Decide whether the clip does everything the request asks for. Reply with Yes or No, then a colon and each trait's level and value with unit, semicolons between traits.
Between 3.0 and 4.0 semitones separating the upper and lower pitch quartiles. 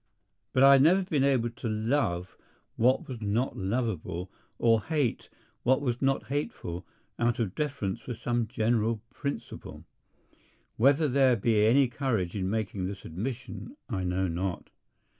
No: average, 5.2 semitones